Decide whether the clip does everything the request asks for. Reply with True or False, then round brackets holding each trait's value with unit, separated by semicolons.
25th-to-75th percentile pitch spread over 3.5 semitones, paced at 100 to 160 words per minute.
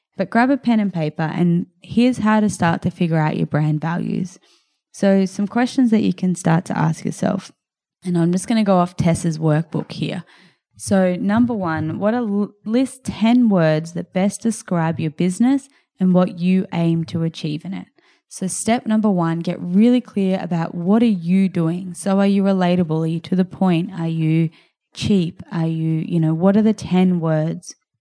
False (3.9 semitones; 195 wpm)